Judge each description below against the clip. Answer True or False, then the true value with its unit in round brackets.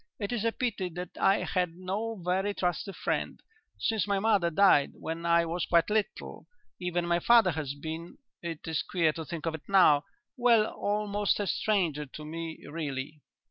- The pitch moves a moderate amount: True (3.9 semitones)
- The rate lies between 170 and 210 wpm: True (180 wpm)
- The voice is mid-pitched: True (180 Hz)